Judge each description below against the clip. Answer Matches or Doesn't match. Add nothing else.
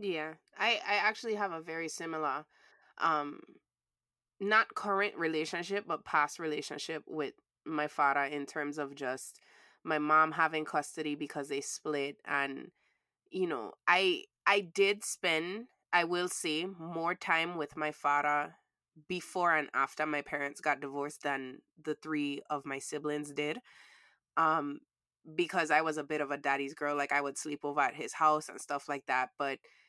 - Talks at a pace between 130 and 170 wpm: Matches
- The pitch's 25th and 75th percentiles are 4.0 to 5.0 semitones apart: Doesn't match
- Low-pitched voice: Doesn't match